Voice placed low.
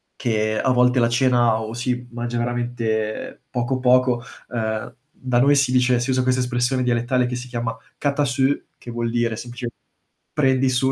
Yes: low, 120 Hz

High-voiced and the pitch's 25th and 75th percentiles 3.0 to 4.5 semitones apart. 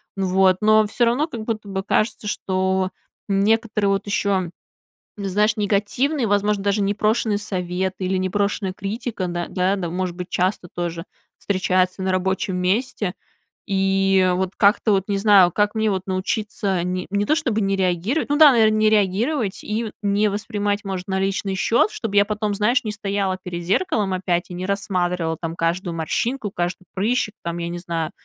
No: high, 195 Hz; narrow, 2.4 semitones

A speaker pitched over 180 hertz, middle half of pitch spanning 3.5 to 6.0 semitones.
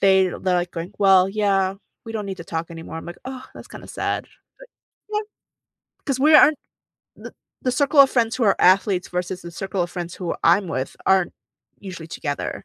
Yes: high, 190 Hz; average, 4.0 semitones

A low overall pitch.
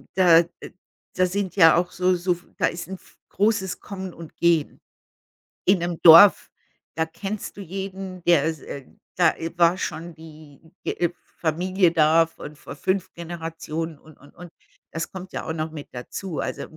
No: medium, 170 Hz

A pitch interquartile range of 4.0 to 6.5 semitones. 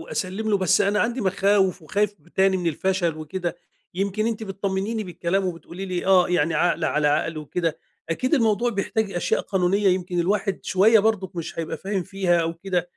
No: average, 2.7 semitones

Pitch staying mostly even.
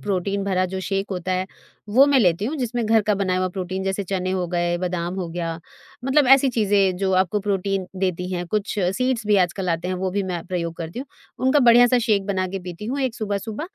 No: average, 3.0 semitones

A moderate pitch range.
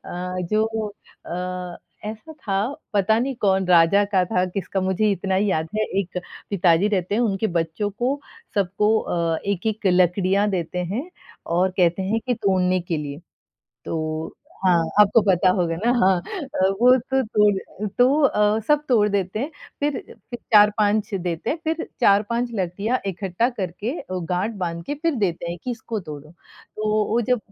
Yes: average, 3.5 semitones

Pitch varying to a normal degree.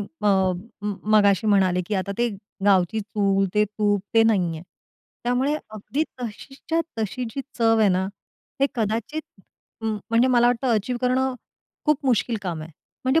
Yes: average, 3.8 semitones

